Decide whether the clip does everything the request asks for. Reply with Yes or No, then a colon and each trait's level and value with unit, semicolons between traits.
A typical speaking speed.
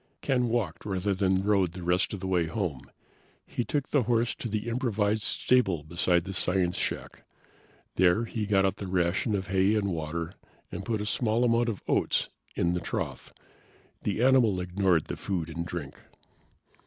Yes: average, 180 wpm